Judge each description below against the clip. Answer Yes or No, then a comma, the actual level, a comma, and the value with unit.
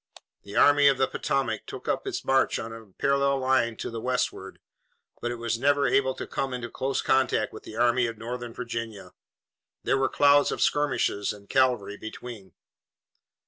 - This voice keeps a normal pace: Yes, average, 180 wpm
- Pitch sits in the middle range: No, low, 125 Hz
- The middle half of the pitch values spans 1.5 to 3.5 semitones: Yes, average, 2.9 semitones